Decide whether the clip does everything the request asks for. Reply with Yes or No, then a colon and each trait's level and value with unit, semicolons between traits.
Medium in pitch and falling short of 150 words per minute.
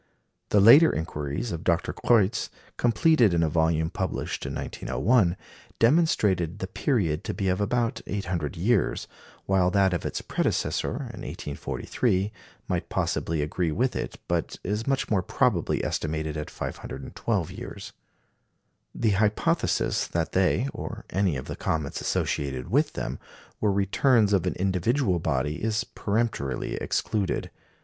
No: very low, 95 Hz; average, 140 wpm